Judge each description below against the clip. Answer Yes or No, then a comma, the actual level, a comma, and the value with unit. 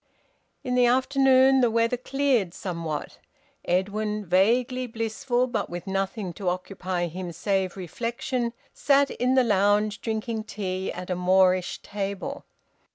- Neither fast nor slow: No, slow, 130 wpm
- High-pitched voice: Yes, high, 210 Hz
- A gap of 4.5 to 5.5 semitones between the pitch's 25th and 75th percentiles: Yes, average, 4.9 semitones